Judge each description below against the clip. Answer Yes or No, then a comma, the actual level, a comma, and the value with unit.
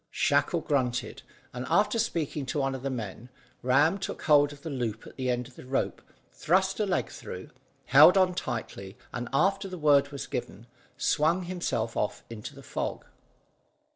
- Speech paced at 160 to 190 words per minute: Yes, average, 175 wpm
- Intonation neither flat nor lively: No, wide, 6.1 semitones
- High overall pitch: No, medium, 140 Hz